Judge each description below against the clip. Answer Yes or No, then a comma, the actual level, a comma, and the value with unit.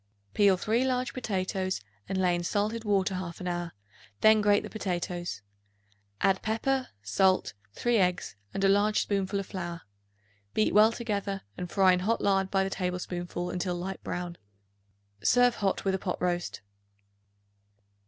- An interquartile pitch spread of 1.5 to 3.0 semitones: Yes, average, 2.7 semitones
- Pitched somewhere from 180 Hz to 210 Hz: Yes, high, 190 Hz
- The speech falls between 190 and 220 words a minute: No, average, 155 wpm